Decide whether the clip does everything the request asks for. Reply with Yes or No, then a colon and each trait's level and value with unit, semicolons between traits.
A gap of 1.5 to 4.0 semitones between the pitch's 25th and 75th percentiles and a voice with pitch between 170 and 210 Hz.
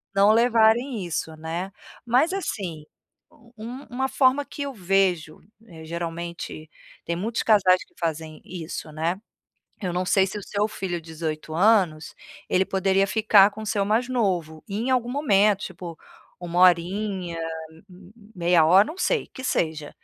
No: average, 4.6 semitones; high, 190 Hz